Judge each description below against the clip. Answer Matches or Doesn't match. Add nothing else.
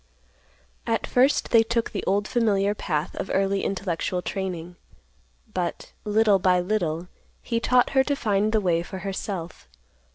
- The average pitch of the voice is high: Matches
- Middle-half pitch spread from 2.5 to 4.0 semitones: Matches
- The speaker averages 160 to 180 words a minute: Doesn't match